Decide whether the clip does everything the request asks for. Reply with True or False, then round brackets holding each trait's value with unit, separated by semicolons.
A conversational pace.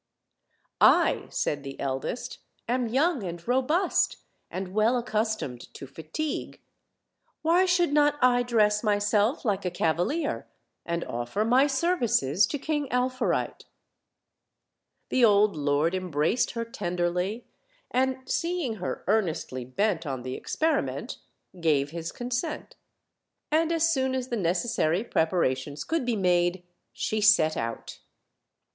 False (125 wpm)